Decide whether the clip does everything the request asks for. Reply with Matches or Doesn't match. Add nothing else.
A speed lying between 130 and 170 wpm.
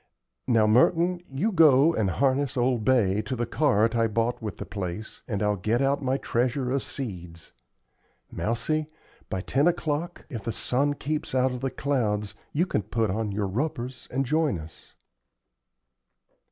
Matches